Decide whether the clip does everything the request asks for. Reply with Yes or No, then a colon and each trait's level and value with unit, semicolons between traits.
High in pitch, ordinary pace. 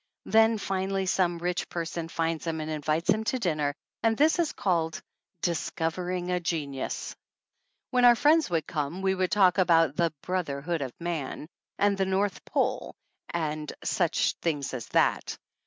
No: medium, 175 Hz; average, 175 wpm